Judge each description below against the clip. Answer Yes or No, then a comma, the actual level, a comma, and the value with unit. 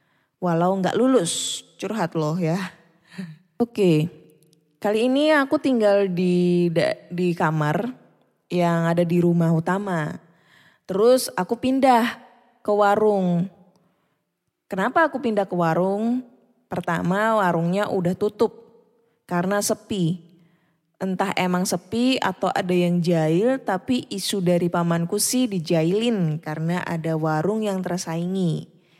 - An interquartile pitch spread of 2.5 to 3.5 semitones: No, average, 4.0 semitones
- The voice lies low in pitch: No, medium, 185 Hz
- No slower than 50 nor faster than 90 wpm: No, average, 110 wpm